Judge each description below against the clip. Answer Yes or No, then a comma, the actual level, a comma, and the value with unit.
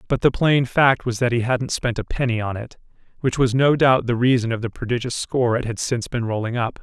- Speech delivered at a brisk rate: Yes, fast, 255 wpm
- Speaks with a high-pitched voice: No, low, 120 Hz